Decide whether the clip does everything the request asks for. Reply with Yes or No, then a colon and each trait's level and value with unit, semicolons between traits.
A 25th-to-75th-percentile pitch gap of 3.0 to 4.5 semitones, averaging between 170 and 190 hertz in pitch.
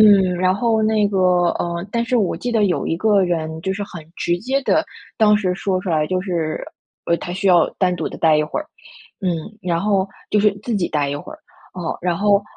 Yes: average, 3.3 semitones; medium, 185 Hz